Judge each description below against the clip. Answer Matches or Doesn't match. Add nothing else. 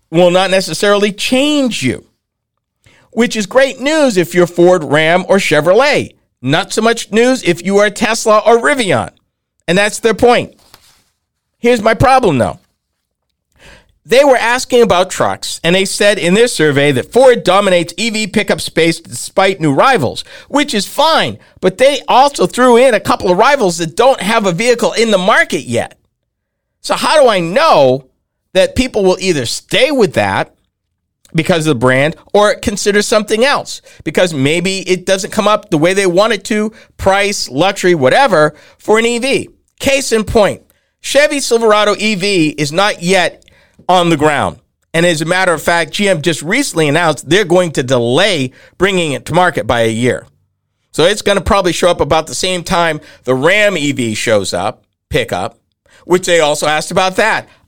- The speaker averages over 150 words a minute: Matches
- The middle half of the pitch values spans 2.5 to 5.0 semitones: Doesn't match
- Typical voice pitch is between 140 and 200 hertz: Matches